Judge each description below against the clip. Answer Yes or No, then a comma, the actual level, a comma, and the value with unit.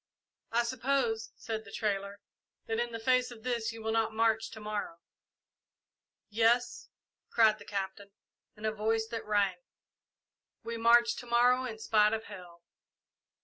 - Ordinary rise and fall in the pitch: No, narrow, 1.9 semitones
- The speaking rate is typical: Yes, average, 150 wpm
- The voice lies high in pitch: Yes, high, 225 Hz